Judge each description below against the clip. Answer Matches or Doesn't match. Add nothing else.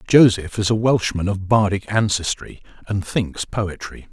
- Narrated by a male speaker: Matches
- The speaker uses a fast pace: Doesn't match